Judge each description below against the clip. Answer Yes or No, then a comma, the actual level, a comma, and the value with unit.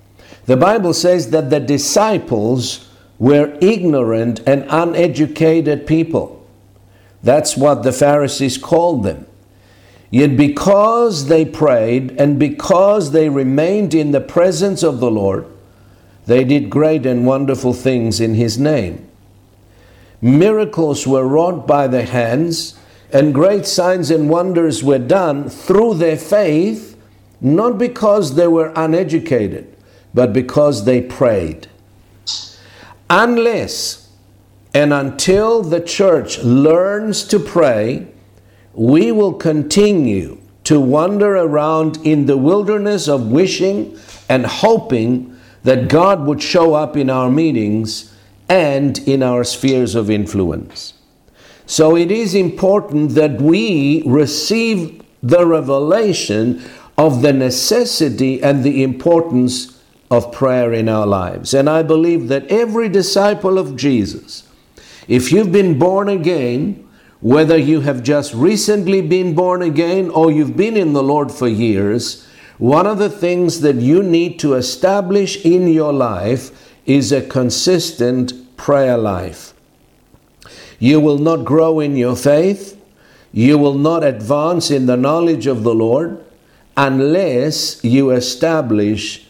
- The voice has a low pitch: No, medium, 145 Hz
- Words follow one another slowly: Yes, slow, 125 wpm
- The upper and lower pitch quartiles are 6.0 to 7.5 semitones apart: No, wide, 5.6 semitones